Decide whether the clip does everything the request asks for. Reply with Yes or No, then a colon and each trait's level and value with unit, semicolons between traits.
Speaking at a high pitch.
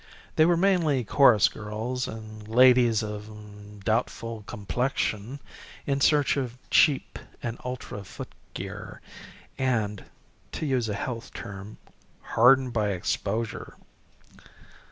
No: low, 115 Hz